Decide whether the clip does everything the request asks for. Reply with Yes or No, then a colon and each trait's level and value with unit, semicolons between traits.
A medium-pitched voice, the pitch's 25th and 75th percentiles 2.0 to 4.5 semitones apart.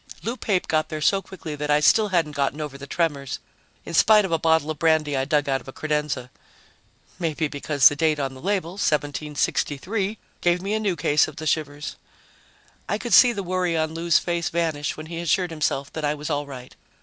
Yes: medium, 155 Hz; average, 3.1 semitones